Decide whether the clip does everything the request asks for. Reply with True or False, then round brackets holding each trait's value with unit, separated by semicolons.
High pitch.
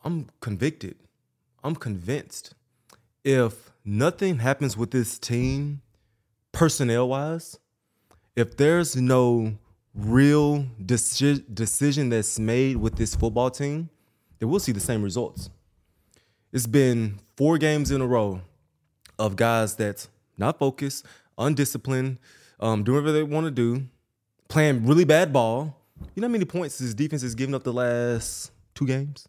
False (125 Hz)